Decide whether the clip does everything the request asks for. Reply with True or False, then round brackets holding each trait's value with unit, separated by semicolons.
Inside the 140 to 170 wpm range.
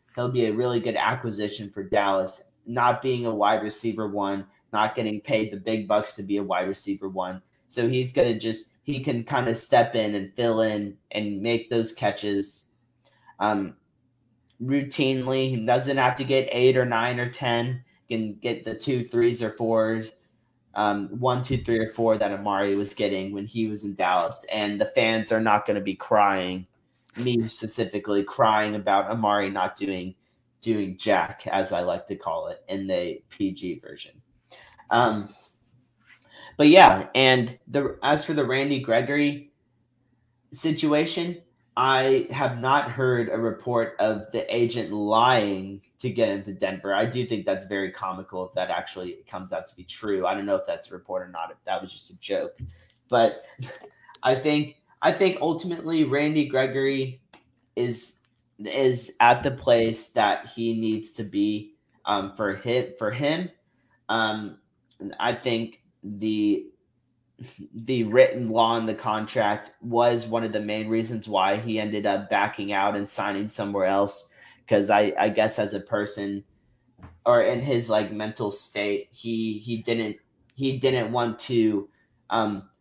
True (165 wpm)